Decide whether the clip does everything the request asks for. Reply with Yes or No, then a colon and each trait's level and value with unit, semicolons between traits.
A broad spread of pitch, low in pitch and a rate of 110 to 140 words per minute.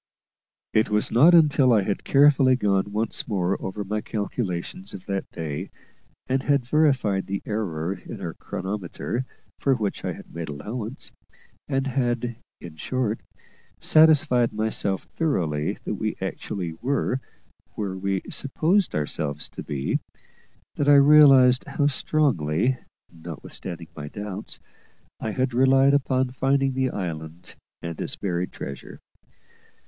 Yes: wide, 6.3 semitones; low, 110 Hz; slow, 135 wpm